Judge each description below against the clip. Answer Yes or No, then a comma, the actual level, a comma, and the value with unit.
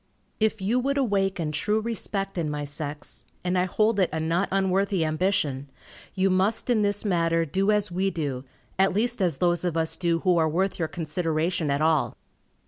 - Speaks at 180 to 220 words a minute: Yes, average, 190 wpm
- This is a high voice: No, medium, 180 Hz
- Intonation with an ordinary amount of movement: Yes, average, 3.6 semitones